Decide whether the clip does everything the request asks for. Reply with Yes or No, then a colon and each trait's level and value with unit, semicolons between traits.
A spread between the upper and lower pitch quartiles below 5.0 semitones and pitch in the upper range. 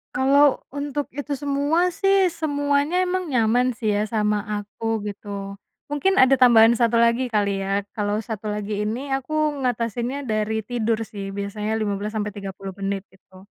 No: average, 5.3 semitones; high, 230 Hz